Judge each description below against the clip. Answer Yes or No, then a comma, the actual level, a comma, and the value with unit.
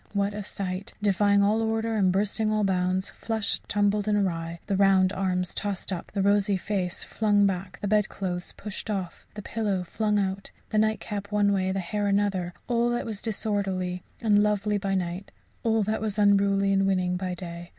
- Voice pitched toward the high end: Yes, high, 200 Hz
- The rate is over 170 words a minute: Yes, average, 185 wpm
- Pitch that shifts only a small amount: Yes, narrow, 1.9 semitones